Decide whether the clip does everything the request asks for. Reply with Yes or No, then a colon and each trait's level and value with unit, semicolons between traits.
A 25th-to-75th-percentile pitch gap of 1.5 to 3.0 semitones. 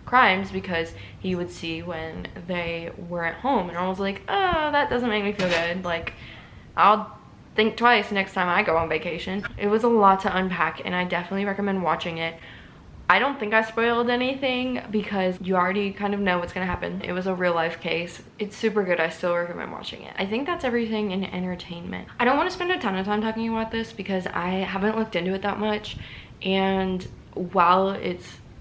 No: average, 3.8 semitones